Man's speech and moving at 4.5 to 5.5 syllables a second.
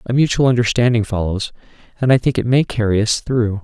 No: male; 5.9 syllables/s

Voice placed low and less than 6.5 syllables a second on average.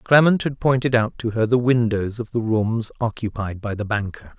Yes: low, 115 Hz; 5.0 syllables/s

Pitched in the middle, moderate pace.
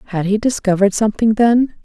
No: high, 215 Hz; average, 165 wpm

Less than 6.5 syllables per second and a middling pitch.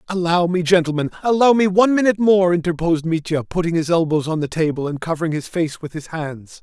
Yes: 6.2 syllables/s; medium, 170 Hz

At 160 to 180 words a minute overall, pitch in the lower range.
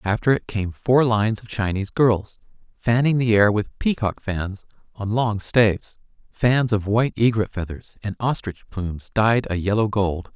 Yes: average, 170 wpm; low, 110 Hz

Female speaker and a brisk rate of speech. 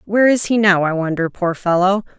Yes: female; fast, 220 wpm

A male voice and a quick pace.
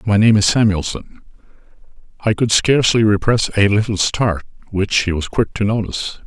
No: male; average, 165 wpm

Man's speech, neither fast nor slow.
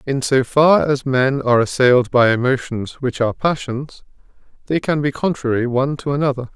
Yes: male; average, 175 wpm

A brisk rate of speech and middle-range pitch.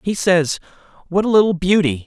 No: average, 175 wpm; medium, 180 Hz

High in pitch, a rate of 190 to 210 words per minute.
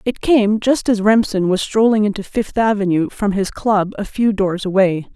Yes: high, 205 Hz; average, 200 wpm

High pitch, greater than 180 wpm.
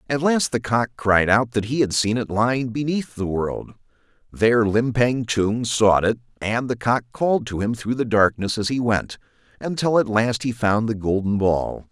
No: low, 115 Hz; average, 200 wpm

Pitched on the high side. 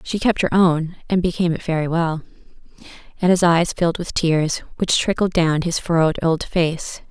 No: medium, 170 Hz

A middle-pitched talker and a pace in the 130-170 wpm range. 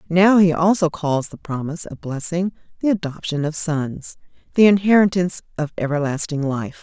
Yes: medium, 165 Hz; average, 150 wpm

